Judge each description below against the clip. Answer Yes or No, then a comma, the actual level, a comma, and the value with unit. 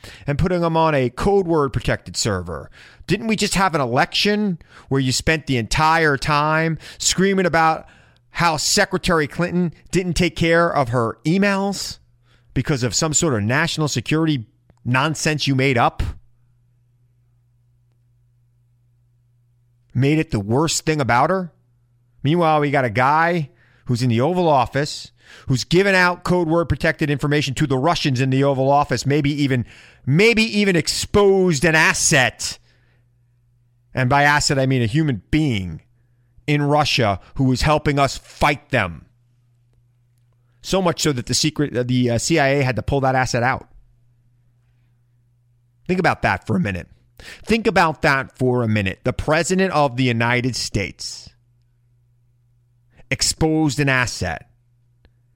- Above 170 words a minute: No, average, 145 wpm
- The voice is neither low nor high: No, low, 130 Hz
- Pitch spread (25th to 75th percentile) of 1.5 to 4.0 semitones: No, average, 4.7 semitones